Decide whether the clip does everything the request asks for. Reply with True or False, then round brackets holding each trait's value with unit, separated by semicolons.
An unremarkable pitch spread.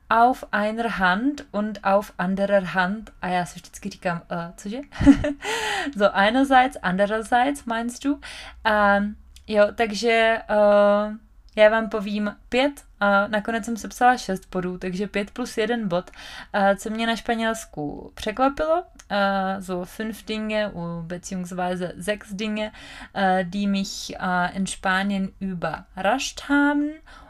True (3.3 semitones)